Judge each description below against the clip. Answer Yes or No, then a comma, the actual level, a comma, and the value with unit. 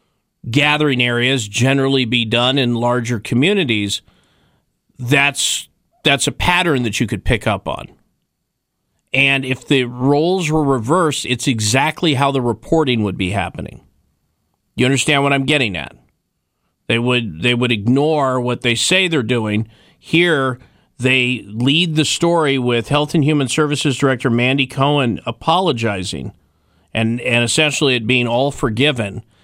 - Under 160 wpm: Yes, average, 140 wpm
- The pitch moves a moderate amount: Yes, average, 3.6 semitones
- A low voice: Yes, low, 130 Hz